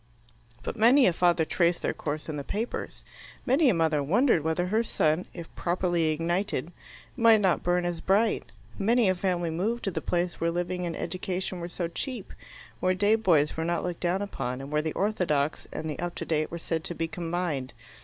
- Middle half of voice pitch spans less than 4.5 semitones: Yes, average, 3.2 semitones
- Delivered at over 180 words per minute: Yes, fast, 205 wpm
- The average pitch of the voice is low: No, medium, 175 Hz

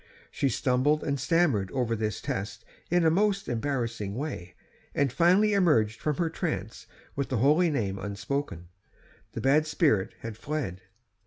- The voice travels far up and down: Yes, wide, 6.5 semitones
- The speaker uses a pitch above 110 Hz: Yes, low, 135 Hz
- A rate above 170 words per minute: No, average, 150 wpm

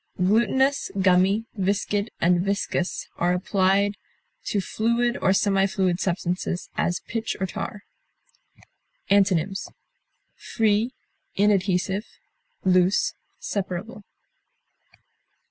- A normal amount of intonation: No, narrow, 2.2 semitones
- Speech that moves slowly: Yes, slow, 85 wpm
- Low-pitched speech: No, high, 195 Hz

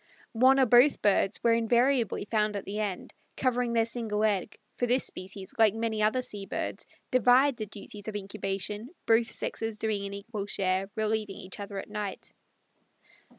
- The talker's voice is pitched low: No, high, 215 Hz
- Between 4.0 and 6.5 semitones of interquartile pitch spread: No, average, 2.7 semitones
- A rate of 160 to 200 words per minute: Yes, average, 170 wpm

